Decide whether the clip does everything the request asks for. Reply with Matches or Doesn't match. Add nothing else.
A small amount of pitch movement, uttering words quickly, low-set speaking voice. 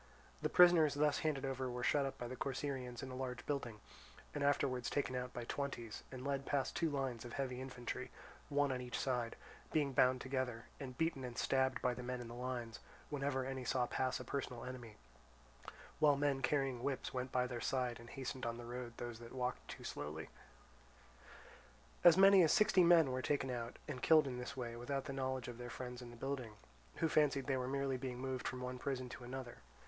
Matches